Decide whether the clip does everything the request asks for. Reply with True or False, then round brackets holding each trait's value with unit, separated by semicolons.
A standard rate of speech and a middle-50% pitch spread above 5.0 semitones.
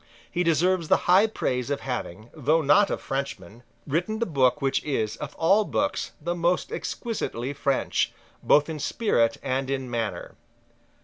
True (160 wpm; 5.5 semitones)